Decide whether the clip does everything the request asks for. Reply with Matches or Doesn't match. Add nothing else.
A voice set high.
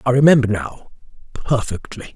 Doesn't match